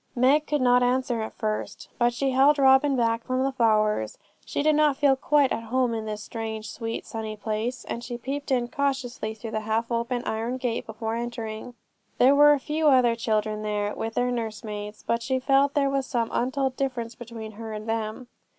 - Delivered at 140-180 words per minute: No, average, 200 wpm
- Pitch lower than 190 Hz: No, high, 240 Hz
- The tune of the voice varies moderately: Yes, average, 3.2 semitones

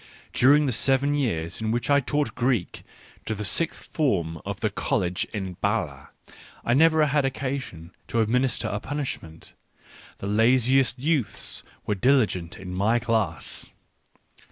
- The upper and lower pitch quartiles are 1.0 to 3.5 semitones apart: No, wide, 5.6 semitones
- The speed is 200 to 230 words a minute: No, average, 140 wpm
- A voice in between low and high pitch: No, low, 120 Hz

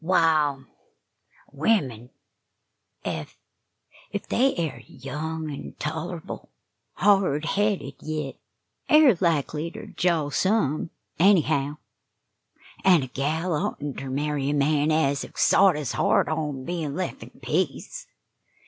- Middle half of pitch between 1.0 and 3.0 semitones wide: No, average, 3.7 semitones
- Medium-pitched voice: Yes, medium, 155 Hz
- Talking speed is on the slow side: Yes, slow, 120 wpm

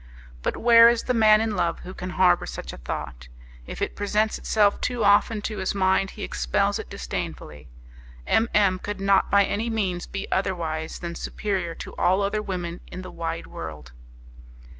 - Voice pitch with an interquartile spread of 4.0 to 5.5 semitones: No, average, 3.6 semitones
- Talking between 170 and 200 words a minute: Yes, average, 180 wpm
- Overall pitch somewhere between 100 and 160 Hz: No, high, 190 Hz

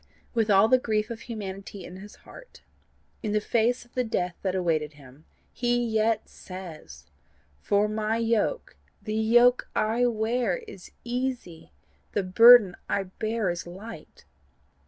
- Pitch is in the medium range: No, high, 215 Hz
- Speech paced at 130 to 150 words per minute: Yes, average, 145 wpm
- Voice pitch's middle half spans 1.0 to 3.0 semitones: No, average, 3.9 semitones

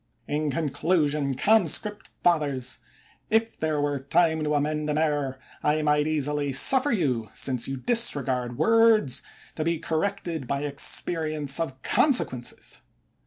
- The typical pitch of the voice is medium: Yes, medium, 150 Hz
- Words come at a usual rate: No, slow, 125 wpm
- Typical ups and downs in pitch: Yes, average, 3.3 semitones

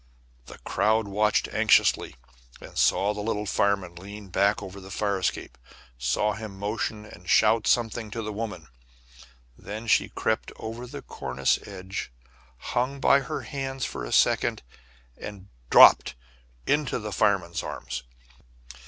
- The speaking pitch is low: Yes, low, 105 Hz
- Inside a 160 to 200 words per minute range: No, average, 145 wpm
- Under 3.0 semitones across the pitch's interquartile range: Yes, narrow, 2.4 semitones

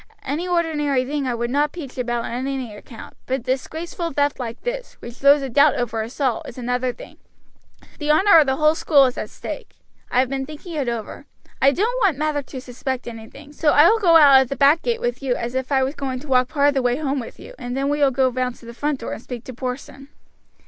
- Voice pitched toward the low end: No, very high, 270 Hz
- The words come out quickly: Yes, fast, 255 wpm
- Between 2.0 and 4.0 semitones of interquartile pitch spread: Yes, average, 3.1 semitones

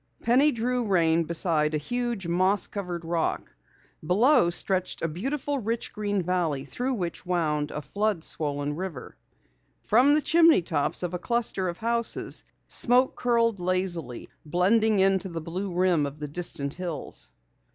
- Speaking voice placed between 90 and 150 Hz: No, medium, 185 Hz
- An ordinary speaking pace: Yes, average, 150 wpm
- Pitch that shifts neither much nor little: No, wide, 5.7 semitones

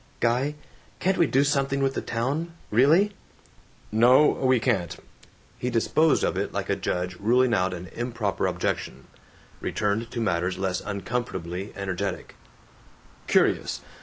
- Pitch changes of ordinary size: No, wide, 5.8 semitones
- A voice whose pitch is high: No, low, 115 Hz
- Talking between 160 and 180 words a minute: No, slow, 135 wpm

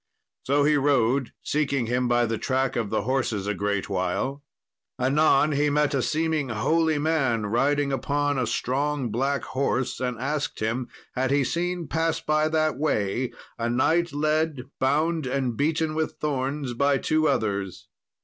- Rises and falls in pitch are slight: No, average, 3.8 semitones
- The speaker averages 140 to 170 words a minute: Yes, average, 160 wpm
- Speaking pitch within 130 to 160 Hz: Yes, medium, 140 Hz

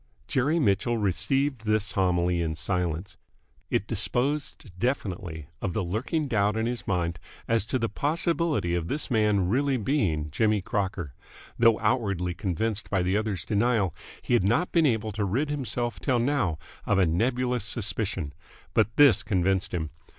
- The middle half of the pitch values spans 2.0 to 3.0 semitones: No, average, 5.1 semitones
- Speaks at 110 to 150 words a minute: No, average, 160 wpm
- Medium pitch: No, low, 105 Hz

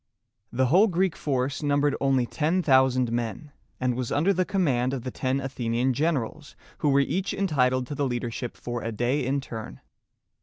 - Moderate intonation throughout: Yes, average, 3.3 semitones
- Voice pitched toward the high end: No, low, 135 Hz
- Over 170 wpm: Yes, average, 180 wpm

